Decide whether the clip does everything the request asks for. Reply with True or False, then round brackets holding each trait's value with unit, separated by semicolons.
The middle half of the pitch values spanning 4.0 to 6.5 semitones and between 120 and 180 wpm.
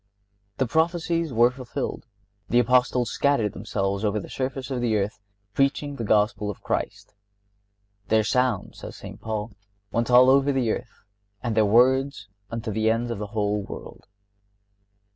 False (3.6 semitones; 155 wpm)